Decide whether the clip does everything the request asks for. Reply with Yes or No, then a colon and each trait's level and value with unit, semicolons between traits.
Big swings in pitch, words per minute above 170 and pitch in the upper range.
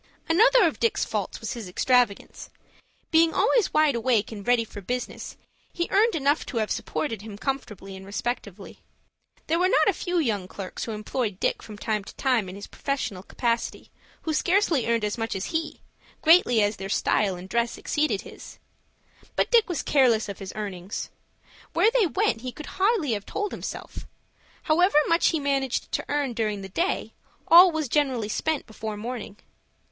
Yes: wide, 7.4 semitones; average, 180 wpm; high, 245 Hz